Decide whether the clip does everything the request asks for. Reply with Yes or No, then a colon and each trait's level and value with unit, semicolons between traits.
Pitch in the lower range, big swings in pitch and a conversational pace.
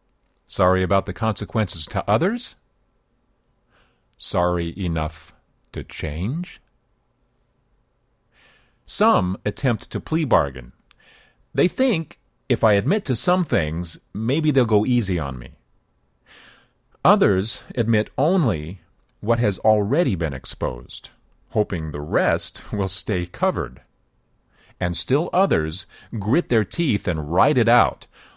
No: low, 105 Hz; wide, 6.0 semitones; slow, 110 wpm